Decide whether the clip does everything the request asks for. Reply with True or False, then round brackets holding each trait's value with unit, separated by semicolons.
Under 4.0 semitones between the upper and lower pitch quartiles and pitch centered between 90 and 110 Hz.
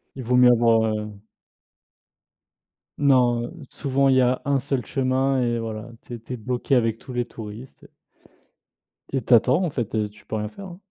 False (2.9 semitones; 125 Hz)